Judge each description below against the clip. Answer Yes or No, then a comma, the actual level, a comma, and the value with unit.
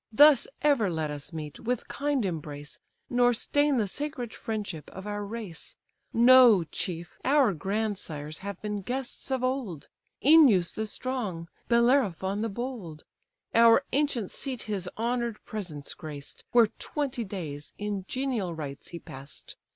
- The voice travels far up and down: Yes, wide, 6.5 semitones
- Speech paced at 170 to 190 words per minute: No, average, 140 wpm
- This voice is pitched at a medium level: No, high, 215 Hz